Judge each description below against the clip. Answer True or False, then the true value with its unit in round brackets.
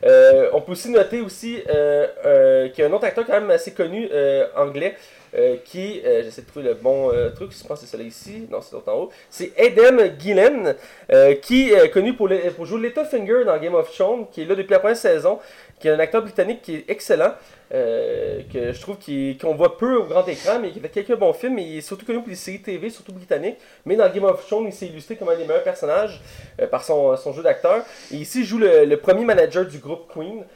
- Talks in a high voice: True (235 Hz)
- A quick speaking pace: True (255 wpm)